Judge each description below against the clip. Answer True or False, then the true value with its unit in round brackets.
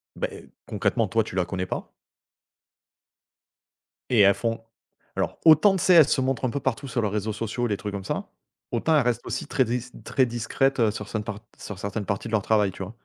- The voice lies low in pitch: True (115 Hz)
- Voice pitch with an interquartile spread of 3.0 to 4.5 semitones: True (4.0 semitones)